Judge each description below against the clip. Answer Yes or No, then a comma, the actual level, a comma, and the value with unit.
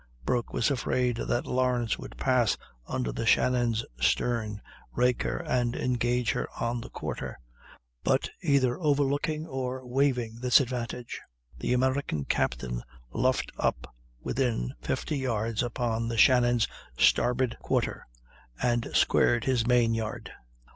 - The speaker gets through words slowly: Yes, slow, 125 wpm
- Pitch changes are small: Yes, narrow, 1.9 semitones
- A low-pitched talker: Yes, low, 120 Hz